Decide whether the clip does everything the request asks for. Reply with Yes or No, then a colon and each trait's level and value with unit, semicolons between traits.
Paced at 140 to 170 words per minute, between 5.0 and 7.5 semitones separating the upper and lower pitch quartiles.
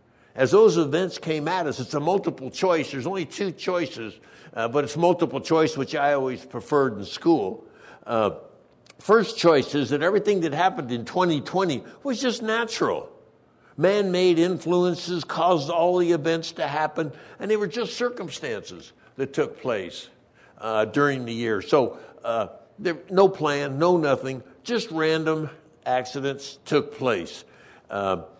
Yes: average, 150 wpm; wide, 5.4 semitones